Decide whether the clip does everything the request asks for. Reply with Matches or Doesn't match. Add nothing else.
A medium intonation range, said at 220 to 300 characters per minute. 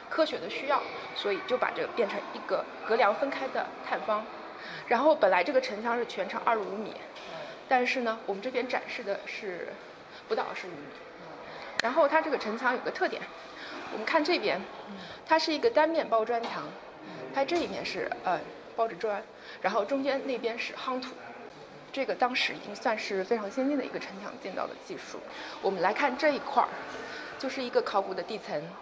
Matches